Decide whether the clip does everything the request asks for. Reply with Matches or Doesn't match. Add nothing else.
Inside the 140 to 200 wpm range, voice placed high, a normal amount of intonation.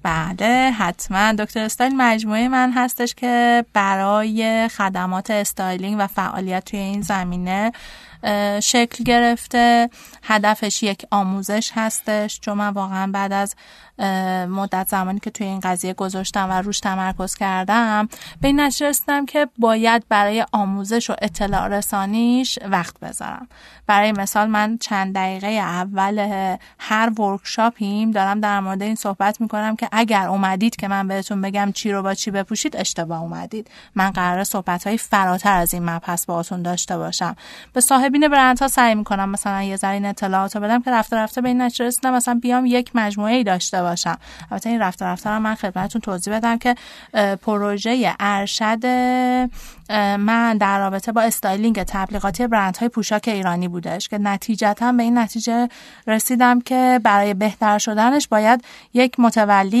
Matches